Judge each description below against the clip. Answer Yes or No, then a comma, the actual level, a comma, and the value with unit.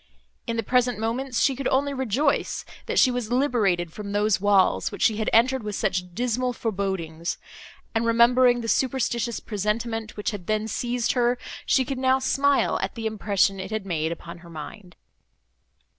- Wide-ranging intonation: No, average, 3.9 semitones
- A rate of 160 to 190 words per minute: Yes, average, 175 wpm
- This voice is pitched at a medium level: No, high, 225 Hz